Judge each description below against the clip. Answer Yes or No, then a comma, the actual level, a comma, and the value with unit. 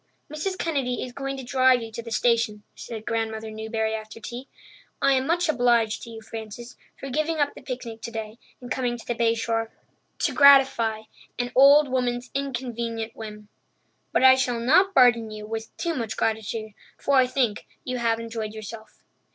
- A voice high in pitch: Yes, high, 235 Hz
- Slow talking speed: No, average, 180 wpm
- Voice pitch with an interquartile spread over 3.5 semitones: No, average, 2.8 semitones